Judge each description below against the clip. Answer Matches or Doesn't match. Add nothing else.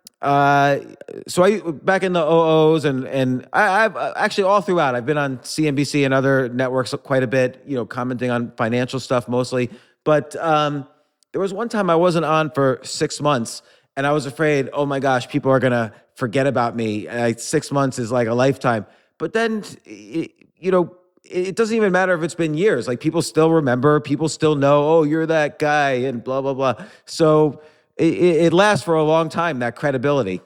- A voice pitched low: Doesn't match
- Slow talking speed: Doesn't match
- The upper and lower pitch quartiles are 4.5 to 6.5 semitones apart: Doesn't match